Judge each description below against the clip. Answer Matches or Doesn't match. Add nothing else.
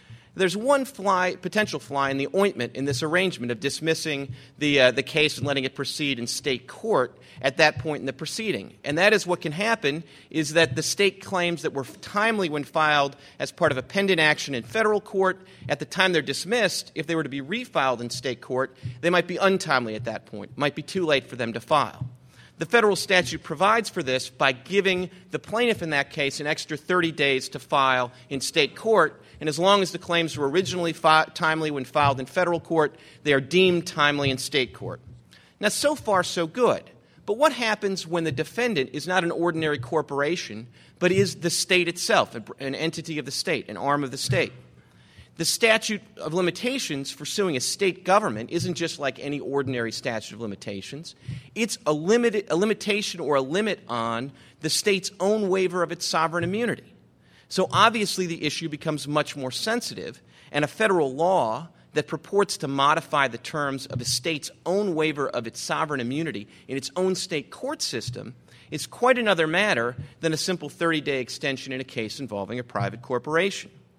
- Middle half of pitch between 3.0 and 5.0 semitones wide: Doesn't match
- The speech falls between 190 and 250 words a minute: Matches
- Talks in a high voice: Doesn't match